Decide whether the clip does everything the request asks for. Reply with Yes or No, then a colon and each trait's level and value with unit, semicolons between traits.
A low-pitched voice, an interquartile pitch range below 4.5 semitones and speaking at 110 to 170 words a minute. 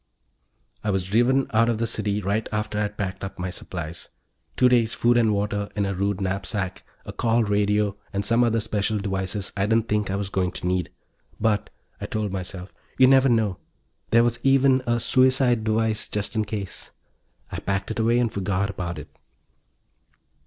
No: low, 105 Hz; average, 2.8 semitones; average, 185 wpm